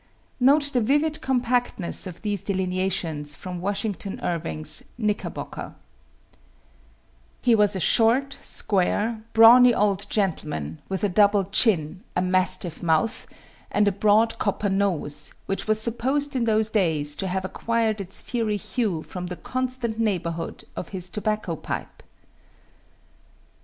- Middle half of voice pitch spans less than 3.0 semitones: No, average, 4.0 semitones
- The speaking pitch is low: No, high, 205 Hz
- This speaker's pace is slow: Yes, slow, 130 wpm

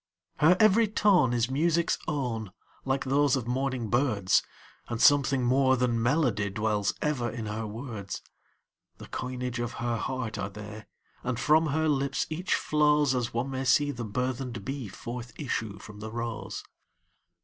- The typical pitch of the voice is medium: No, low, 125 Hz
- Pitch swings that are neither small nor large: Yes, average, 3.7 semitones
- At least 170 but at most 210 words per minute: No, average, 150 wpm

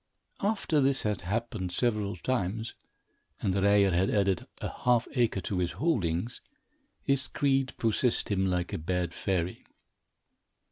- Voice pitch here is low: Yes, low, 100 Hz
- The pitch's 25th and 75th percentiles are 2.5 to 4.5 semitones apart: No, average, 5.2 semitones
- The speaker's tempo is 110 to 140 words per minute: Yes, slow, 135 wpm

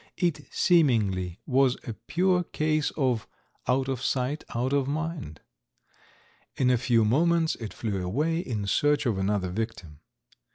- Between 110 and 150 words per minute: Yes, average, 140 wpm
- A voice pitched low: Yes, low, 130 Hz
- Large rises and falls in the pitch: Yes, wide, 6.3 semitones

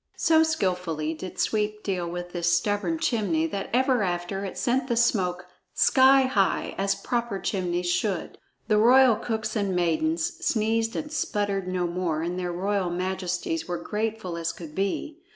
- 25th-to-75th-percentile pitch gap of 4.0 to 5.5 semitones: Yes, average, 4.4 semitones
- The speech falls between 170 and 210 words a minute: No, average, 160 wpm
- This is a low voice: No, high, 195 Hz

